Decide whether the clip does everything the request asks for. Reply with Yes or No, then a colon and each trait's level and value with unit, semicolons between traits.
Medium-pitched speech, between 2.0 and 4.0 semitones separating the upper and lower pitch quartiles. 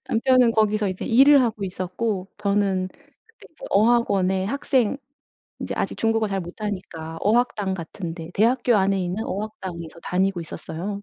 No: high, 200 Hz; average, 3.6 semitones